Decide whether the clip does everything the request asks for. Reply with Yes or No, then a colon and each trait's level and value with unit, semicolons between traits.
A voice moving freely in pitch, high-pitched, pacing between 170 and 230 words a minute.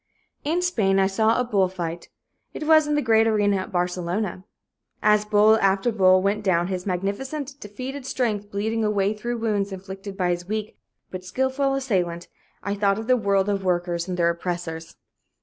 No: average, 3.3 semitones; high, 200 Hz; average, 180 wpm